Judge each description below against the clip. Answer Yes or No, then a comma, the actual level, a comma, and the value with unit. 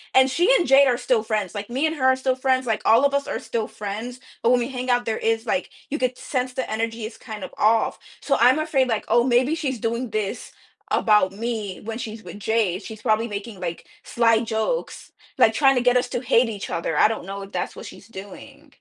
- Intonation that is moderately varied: Yes, average, 3.1 semitones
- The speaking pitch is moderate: No, high, 230 Hz